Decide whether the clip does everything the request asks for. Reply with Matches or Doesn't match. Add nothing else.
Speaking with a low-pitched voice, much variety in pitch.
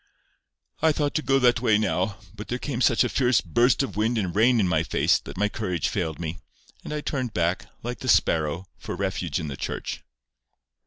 Matches